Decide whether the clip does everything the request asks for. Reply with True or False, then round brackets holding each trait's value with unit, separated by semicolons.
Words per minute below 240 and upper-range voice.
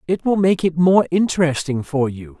False (200 wpm; 165 Hz)